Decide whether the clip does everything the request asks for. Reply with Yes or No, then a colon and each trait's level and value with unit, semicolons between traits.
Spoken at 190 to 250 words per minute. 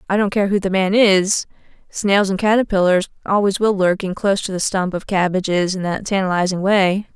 Yes: average, 200 wpm